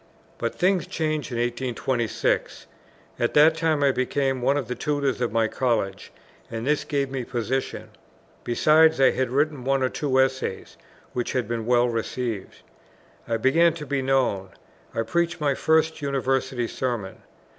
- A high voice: No, low, 130 Hz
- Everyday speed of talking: Yes, average, 155 wpm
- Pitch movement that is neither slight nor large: Yes, average, 3.3 semitones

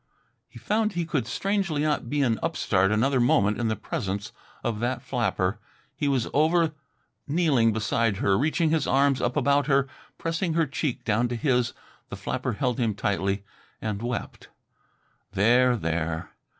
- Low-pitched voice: Yes, low, 125 Hz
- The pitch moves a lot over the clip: Yes, wide, 5.7 semitones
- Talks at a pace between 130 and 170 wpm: Yes, average, 160 wpm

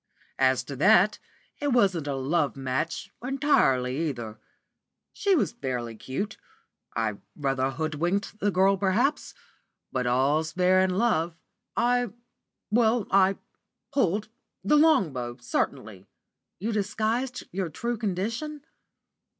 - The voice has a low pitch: No, medium, 185 Hz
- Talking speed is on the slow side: Yes, slow, 120 wpm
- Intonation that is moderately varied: No, wide, 8.5 semitones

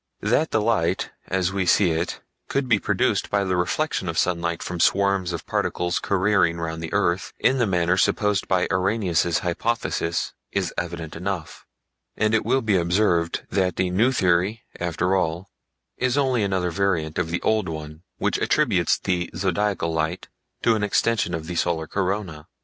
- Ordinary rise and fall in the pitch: Yes, average, 3.4 semitones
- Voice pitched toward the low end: Yes, very low, 90 Hz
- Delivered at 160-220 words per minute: Yes, average, 170 wpm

